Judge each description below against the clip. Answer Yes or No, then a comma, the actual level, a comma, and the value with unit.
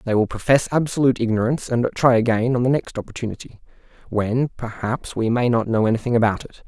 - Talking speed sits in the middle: Yes, average, 190 wpm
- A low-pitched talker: Yes, low, 120 Hz